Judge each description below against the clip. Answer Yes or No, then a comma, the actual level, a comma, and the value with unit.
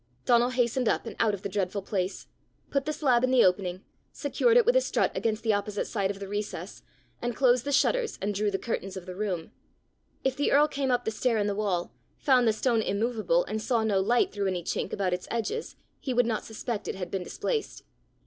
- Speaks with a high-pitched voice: Yes, high, 220 Hz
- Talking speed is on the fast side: Yes, fast, 230 wpm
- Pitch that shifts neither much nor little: Yes, average, 4.2 semitones